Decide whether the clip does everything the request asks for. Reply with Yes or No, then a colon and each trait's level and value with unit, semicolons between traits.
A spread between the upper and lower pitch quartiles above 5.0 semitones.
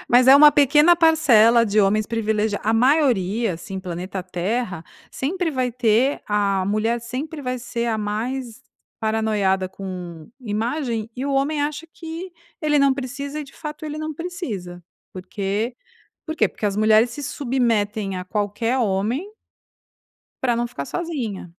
Yes: wide, 5.4 semitones